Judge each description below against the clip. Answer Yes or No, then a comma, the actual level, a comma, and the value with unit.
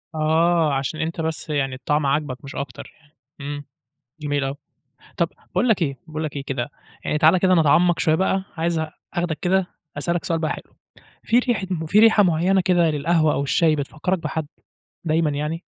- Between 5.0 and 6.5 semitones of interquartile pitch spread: No, average, 3.1 semitones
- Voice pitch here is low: No, medium, 160 Hz